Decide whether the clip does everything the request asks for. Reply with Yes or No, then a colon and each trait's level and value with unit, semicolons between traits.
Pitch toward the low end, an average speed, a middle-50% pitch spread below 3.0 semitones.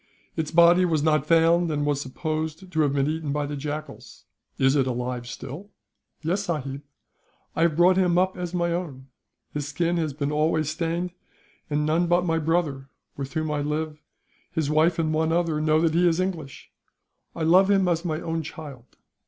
No: medium, 160 Hz; average, 190 wpm; narrow, 2.6 semitones